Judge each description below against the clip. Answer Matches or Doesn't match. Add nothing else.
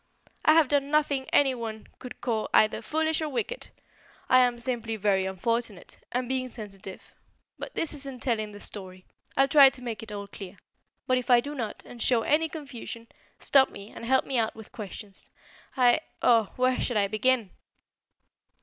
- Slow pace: Doesn't match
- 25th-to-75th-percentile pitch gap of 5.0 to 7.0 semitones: Doesn't match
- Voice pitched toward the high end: Matches